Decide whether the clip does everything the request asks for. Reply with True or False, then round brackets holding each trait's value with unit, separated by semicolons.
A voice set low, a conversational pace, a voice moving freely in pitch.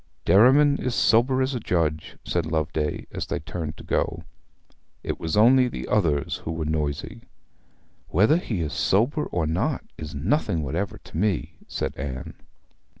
True (85 Hz; 155 wpm; 7.3 semitones)